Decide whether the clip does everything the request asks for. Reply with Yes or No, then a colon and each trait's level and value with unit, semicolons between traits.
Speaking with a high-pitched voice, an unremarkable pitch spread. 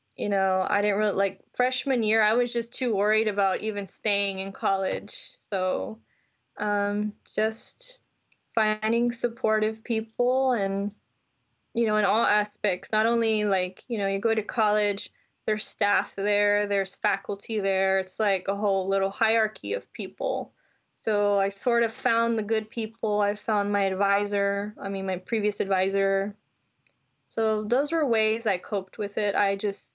No: high, 210 Hz; narrow, 2.0 semitones